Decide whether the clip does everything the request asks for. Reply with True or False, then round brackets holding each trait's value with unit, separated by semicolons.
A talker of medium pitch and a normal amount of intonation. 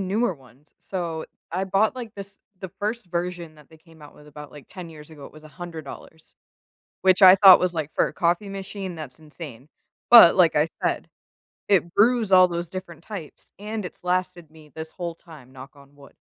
True (170 Hz; 3.7 semitones)